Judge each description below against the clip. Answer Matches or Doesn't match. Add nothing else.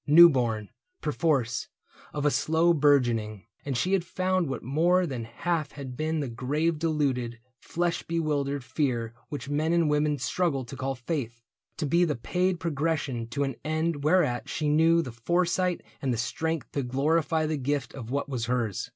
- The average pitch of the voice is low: Doesn't match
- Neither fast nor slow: Matches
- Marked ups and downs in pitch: Doesn't match